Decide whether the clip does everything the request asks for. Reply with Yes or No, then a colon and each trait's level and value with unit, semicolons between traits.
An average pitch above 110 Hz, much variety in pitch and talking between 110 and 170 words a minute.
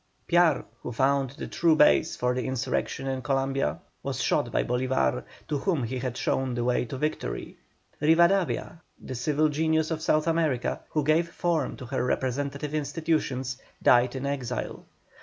No: medium, 140 Hz; average, 3.6 semitones; average, 160 wpm